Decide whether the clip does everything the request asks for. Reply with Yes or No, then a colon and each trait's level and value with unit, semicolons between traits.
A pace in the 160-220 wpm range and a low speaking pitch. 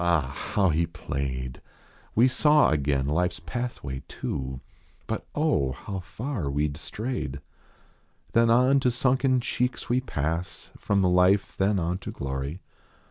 No: average, 140 wpm; very low, 90 Hz